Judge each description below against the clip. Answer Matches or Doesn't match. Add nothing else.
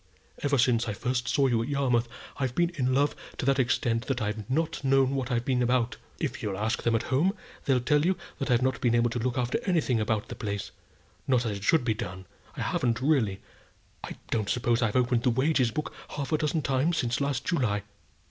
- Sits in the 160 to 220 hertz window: Doesn't match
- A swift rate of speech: Matches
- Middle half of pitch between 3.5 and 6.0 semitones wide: Doesn't match